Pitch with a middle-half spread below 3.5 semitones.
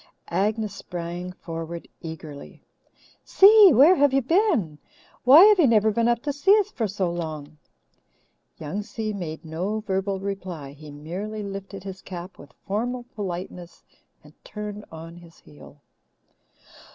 No: average, 5.0 semitones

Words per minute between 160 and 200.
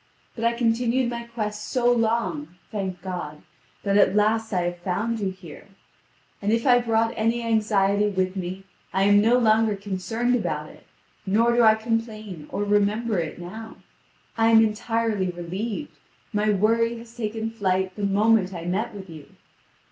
Yes: average, 165 wpm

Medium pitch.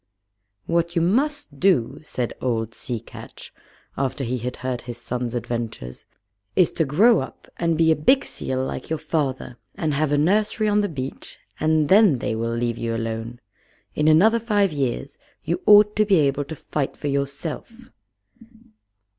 Yes: medium, 145 Hz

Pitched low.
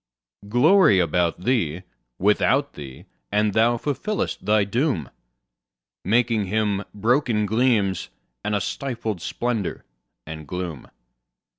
Yes: low, 105 Hz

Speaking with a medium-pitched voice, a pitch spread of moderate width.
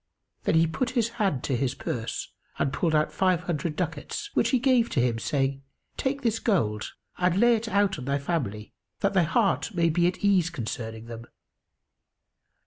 No: medium, 170 Hz; wide, 7.2 semitones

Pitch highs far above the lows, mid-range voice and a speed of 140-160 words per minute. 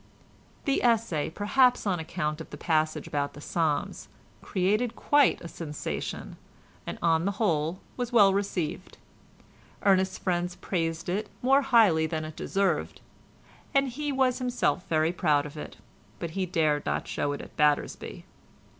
Yes: wide, 5.8 semitones; medium, 180 Hz; average, 150 wpm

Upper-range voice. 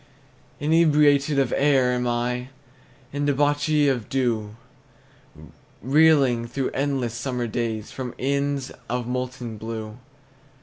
No: low, 130 Hz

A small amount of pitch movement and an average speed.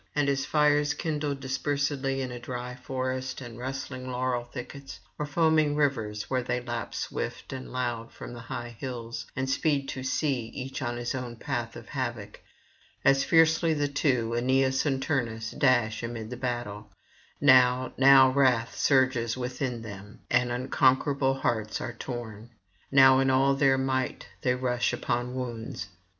Yes: narrow, 2.2 semitones; average, 155 wpm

